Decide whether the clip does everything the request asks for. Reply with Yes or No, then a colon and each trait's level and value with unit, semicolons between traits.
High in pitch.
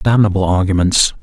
No: low, 100 Hz